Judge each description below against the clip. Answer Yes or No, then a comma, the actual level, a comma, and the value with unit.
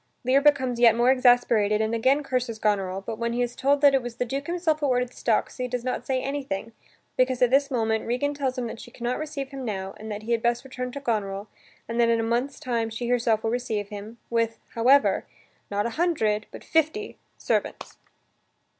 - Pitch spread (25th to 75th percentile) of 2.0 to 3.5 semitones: Yes, average, 3.1 semitones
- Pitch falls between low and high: No, high, 245 Hz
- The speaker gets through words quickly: Yes, fast, 225 wpm